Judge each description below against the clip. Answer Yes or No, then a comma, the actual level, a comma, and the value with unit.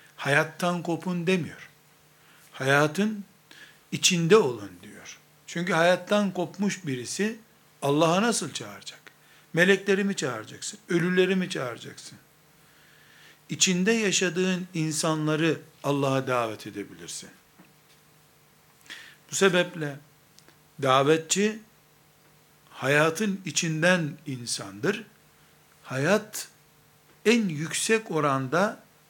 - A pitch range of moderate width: Yes, average, 3.6 semitones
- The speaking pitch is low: No, medium, 160 Hz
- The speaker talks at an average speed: No, slow, 75 wpm